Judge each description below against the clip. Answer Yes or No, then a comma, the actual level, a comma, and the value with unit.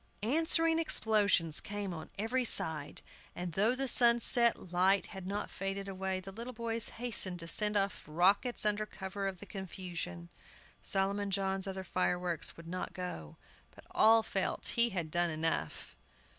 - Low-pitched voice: No, high, 195 Hz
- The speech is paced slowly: No, average, 155 wpm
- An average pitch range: Yes, average, 3.6 semitones